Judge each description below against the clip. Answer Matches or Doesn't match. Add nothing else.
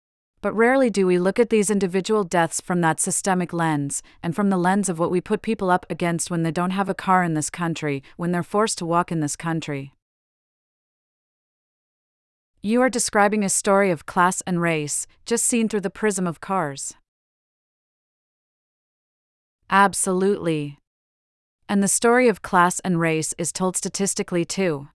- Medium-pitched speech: Matches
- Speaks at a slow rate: Doesn't match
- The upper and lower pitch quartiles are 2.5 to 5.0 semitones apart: Matches